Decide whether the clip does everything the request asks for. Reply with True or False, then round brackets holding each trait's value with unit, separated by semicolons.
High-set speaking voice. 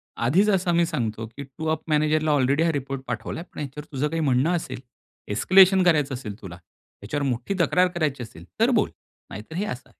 False (145 Hz)